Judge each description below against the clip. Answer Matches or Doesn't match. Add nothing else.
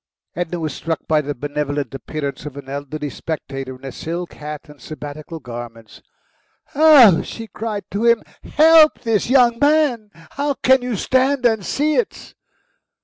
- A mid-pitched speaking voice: Matches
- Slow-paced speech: Doesn't match